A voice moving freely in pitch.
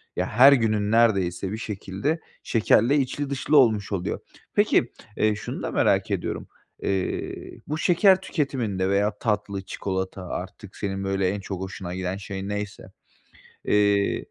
No: average, 3.3 semitones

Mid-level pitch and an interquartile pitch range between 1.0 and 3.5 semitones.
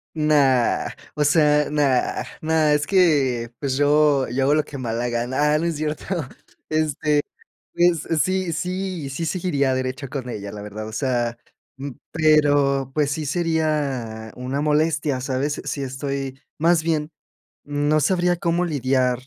Yes: medium, 145 Hz; average, 3.1 semitones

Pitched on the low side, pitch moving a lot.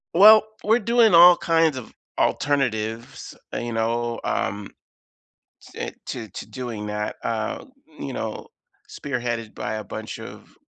Yes: low, 120 Hz; wide, 6.9 semitones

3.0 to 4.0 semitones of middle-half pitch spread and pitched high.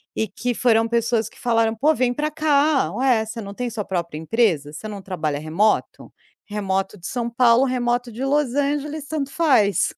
No: average, 4.6 semitones; high, 235 Hz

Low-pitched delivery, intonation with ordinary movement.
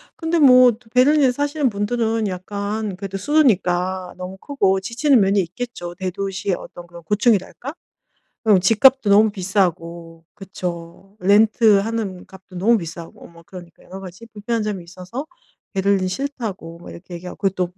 No: high, 195 Hz; average, 4.0 semitones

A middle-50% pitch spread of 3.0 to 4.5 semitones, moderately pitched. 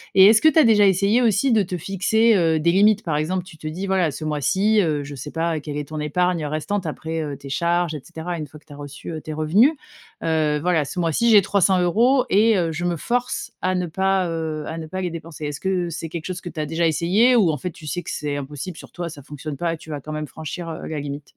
Yes: average, 3.7 semitones; medium, 170 Hz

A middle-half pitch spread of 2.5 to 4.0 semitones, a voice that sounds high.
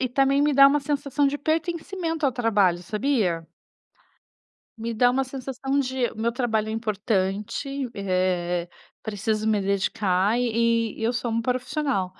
No: average, 4.9 semitones; high, 235 Hz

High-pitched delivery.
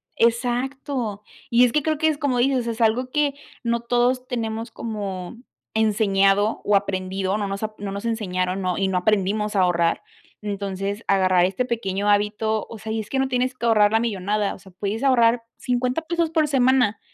Yes: high, 220 Hz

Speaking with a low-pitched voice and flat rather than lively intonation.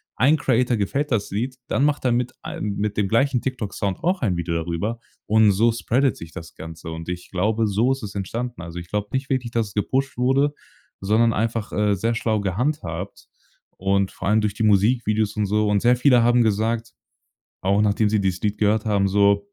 No: low, 105 Hz; average, 3.4 semitones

